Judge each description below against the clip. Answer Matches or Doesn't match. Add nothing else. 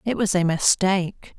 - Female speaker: Matches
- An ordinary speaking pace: Matches